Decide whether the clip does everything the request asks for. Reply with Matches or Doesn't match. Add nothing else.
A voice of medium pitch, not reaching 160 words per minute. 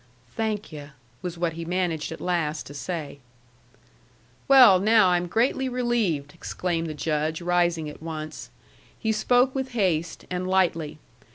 Matches